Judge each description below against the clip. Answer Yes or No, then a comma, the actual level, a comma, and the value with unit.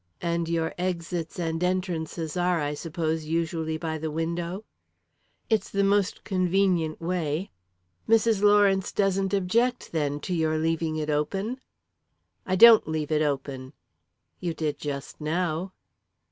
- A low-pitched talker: No, medium, 170 Hz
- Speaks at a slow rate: Yes, slow, 130 wpm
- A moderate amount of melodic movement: Yes, average, 3.1 semitones